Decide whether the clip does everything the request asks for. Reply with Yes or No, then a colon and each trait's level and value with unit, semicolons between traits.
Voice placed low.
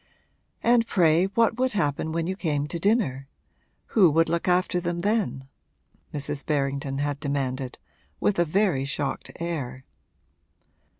No: medium, 160 Hz